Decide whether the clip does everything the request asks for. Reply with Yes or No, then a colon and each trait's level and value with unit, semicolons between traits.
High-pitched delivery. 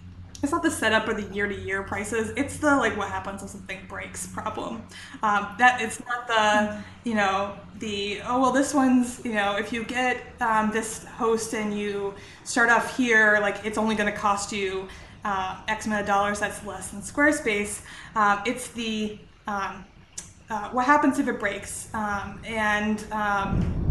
Yes: high, 215 Hz